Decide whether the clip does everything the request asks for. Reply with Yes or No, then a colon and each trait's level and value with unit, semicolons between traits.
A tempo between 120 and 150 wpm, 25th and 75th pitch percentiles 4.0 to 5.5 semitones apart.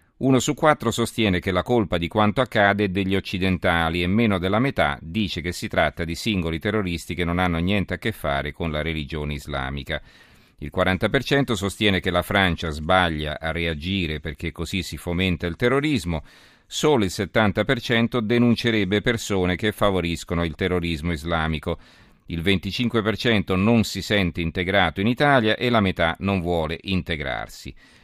No: average, 160 wpm; average, 4.4 semitones